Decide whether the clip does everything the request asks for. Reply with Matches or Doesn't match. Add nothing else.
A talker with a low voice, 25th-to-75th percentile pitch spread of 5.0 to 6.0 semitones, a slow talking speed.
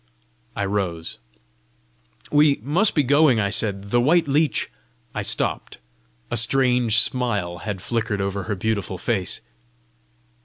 Matches